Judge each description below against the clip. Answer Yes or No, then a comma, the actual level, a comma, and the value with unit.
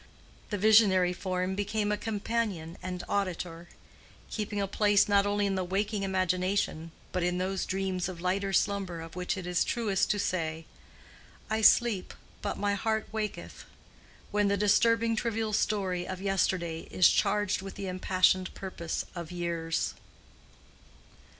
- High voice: Yes, high, 195 Hz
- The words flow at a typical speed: Yes, average, 145 wpm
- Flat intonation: Yes, narrow, 2.3 semitones